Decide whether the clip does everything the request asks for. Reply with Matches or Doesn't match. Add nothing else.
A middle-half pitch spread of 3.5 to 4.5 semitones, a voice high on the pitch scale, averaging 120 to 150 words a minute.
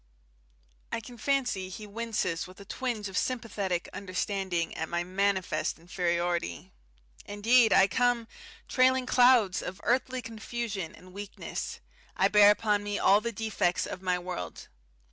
Matches